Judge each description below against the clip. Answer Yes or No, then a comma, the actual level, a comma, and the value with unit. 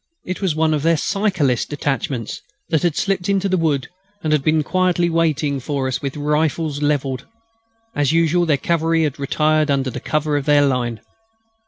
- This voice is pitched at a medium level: Yes, medium, 150 Hz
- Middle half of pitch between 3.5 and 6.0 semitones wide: No, average, 2.9 semitones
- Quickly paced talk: No, average, 175 wpm